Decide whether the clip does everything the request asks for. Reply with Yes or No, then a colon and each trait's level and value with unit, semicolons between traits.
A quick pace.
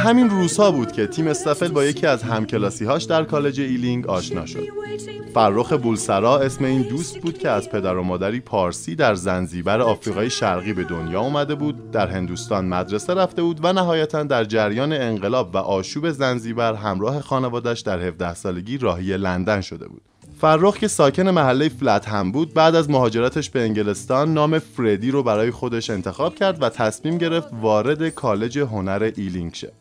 Yes: fast, 170 wpm